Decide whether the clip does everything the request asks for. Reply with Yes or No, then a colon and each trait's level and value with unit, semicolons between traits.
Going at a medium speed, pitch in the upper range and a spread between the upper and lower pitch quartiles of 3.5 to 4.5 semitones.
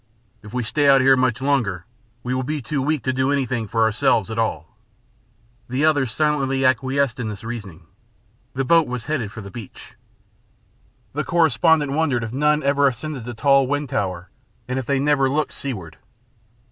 No: average, 185 wpm; low, 130 Hz; average, 4.0 semitones